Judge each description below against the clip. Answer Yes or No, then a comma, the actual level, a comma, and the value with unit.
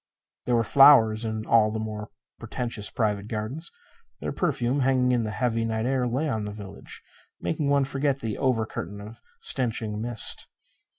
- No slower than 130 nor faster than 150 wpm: No, average, 170 wpm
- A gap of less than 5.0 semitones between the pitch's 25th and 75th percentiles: Yes, average, 3.3 semitones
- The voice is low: Yes, low, 115 Hz